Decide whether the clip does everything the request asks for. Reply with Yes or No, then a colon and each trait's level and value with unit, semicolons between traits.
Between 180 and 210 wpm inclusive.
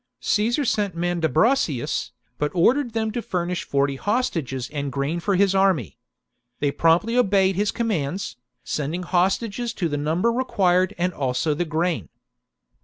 No: average, 145 wpm